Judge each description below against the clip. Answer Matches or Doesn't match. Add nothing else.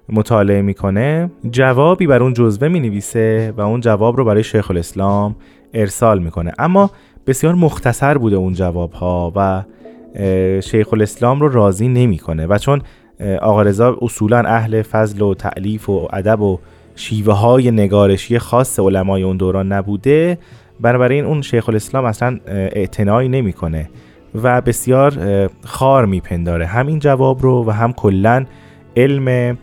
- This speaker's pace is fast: Doesn't match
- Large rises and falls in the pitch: Doesn't match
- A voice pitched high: Doesn't match